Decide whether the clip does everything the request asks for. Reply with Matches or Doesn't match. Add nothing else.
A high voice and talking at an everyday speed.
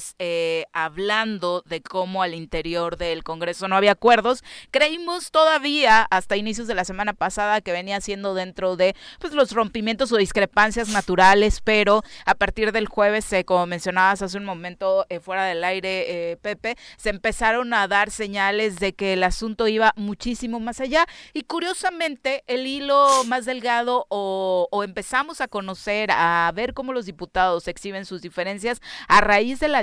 Matches